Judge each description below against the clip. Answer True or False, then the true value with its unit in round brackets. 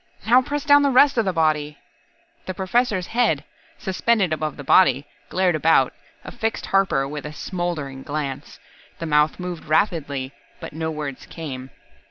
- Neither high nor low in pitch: True (165 Hz)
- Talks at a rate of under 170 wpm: True (155 wpm)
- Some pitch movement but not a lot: True (4.7 semitones)